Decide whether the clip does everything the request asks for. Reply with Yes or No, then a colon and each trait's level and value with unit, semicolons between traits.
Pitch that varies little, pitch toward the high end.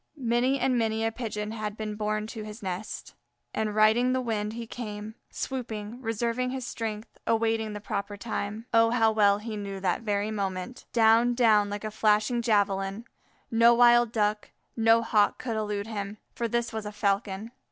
Yes: narrow, 1.9 semitones; high, 220 Hz